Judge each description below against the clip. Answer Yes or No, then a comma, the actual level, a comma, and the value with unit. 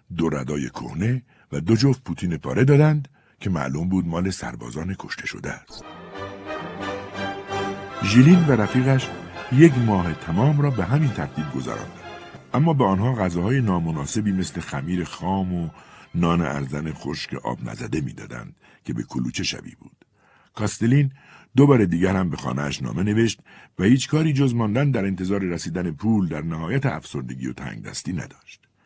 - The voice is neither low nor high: No, low, 100 Hz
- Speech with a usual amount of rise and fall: No, wide, 7.1 semitones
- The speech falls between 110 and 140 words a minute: No, average, 150 wpm